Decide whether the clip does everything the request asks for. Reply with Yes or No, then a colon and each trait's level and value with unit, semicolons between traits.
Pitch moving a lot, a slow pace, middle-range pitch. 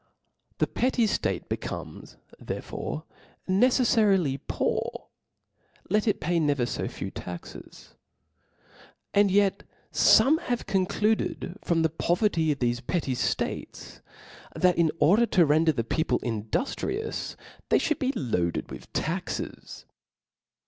Yes: wide, 7.2 semitones; slow, 120 wpm; medium, 175 Hz